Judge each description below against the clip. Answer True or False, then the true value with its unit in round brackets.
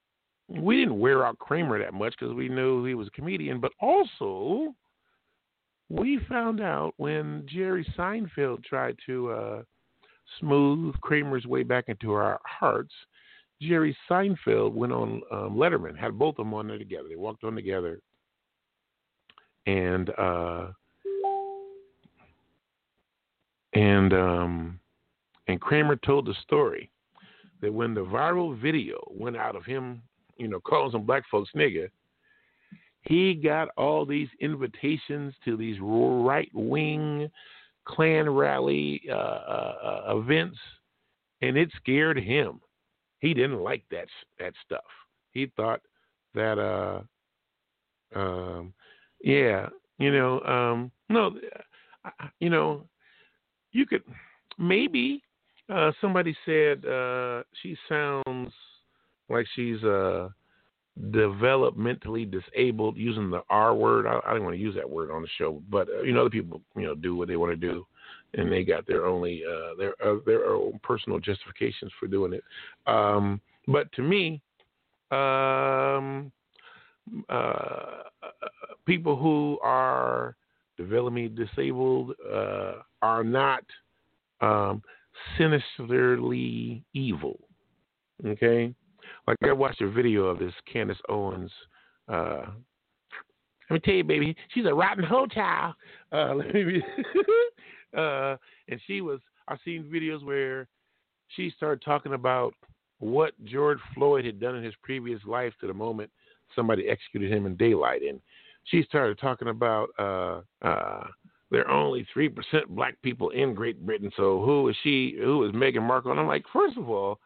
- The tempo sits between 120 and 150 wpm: True (140 wpm)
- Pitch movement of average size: False (7.1 semitones)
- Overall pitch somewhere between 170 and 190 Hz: False (135 Hz)